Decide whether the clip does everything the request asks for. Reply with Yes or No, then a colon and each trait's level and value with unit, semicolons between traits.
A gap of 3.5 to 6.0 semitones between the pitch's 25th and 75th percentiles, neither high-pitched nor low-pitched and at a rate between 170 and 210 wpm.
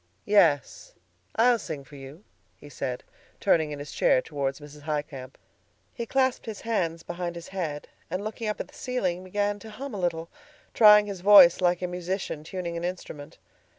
Yes: wide, 5.5 semitones; medium, 175 Hz; average, 180 wpm